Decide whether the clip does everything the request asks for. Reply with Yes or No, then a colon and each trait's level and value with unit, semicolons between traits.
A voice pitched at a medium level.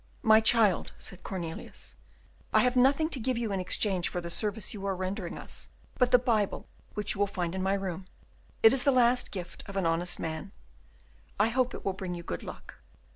No: high, 200 Hz